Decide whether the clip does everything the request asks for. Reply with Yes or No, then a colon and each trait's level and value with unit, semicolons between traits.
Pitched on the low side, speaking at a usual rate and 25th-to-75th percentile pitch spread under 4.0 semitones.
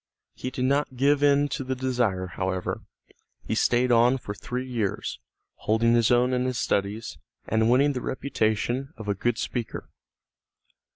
Yes: low, 125 Hz; average, 160 wpm; average, 2.9 semitones